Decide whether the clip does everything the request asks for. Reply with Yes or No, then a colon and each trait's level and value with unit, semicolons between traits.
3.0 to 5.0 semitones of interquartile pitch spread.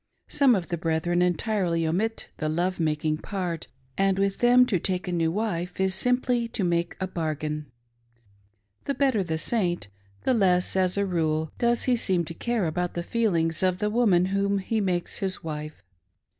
Yes: average, 4.0 semitones